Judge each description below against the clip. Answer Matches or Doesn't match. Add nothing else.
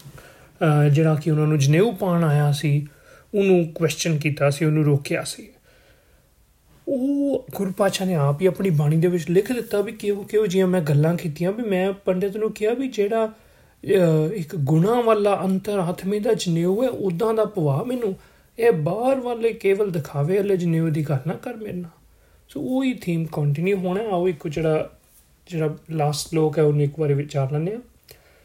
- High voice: Doesn't match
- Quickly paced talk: Matches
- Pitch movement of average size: Matches